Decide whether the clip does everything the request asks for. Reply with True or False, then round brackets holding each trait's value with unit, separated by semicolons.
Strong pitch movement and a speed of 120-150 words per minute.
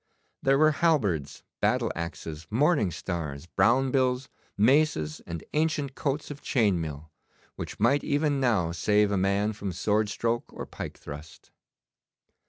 True (8.4 semitones; 140 wpm)